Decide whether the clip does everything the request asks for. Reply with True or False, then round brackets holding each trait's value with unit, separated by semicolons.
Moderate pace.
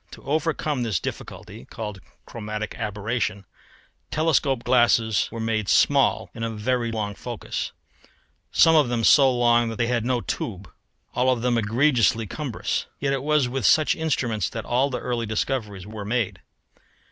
True (160 wpm)